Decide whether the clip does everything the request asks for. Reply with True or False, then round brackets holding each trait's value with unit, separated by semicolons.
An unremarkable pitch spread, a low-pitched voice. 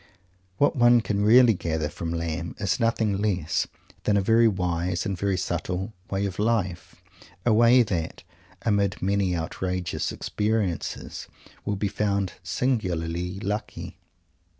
True (3.4 semitones; 100 Hz)